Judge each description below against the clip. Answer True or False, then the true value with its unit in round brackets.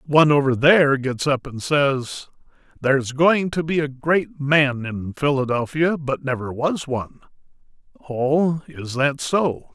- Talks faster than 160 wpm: False (155 wpm)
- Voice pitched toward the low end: False (145 Hz)